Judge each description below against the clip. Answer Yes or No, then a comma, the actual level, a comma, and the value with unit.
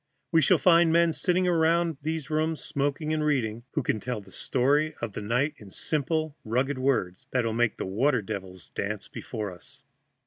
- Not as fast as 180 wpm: No, average, 185 wpm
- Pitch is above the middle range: No, low, 135 Hz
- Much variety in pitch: Yes, wide, 6.1 semitones